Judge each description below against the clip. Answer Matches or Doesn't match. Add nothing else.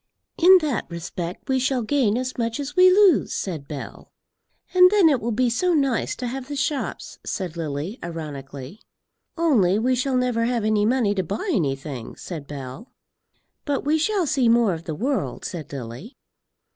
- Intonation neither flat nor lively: Doesn't match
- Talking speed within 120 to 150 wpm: Doesn't match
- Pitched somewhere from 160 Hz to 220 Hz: Doesn't match